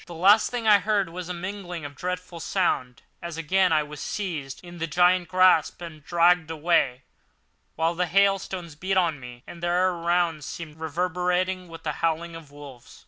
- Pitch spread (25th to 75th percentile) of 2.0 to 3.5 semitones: Yes, narrow, 2.4 semitones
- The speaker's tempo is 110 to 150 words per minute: No, average, 185 wpm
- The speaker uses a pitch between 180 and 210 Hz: No, medium, 170 Hz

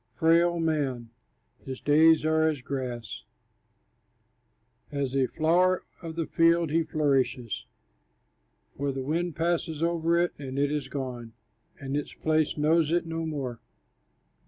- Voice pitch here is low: No, medium, 155 Hz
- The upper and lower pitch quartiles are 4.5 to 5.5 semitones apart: No, average, 3.5 semitones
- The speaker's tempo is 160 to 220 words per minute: No, slow, 135 wpm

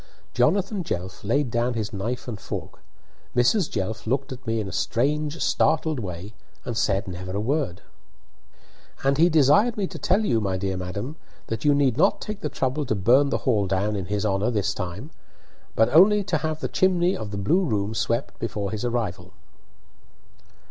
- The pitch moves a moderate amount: No, wide, 6.9 semitones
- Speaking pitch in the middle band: No, low, 120 Hz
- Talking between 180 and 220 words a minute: Yes, average, 185 wpm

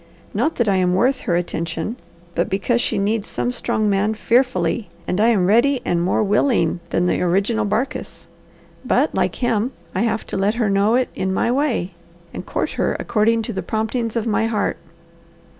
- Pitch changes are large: No, average, 3.5 semitones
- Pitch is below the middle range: No, high, 215 Hz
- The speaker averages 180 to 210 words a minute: Yes, average, 190 wpm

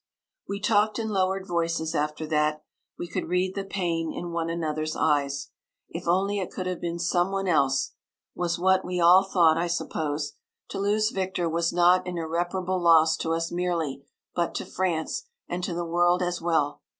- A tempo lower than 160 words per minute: No, average, 185 wpm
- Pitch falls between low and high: Yes, medium, 175 Hz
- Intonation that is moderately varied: No, narrow, 2.3 semitones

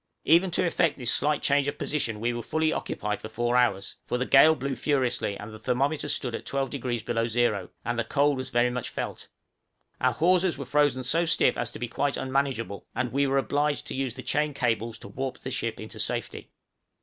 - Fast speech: Yes, fast, 210 wpm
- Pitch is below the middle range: Yes, low, 130 Hz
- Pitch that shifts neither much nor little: Yes, average, 3.5 semitones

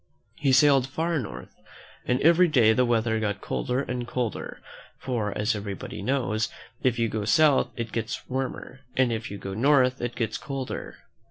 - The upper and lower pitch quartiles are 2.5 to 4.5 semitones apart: Yes, average, 3.3 semitones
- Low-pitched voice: Yes, low, 125 Hz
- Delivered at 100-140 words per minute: No, average, 170 wpm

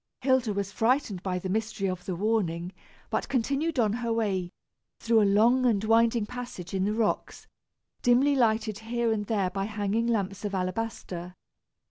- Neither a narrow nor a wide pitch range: Yes, average, 3.1 semitones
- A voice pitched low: No, high, 215 Hz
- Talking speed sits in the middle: Yes, average, 165 wpm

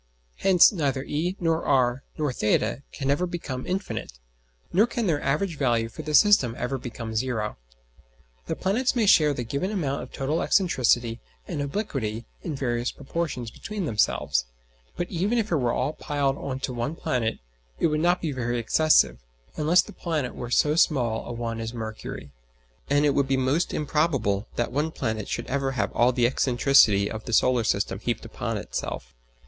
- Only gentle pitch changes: No, average, 5.1 semitones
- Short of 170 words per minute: No, average, 180 wpm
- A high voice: No, low, 135 Hz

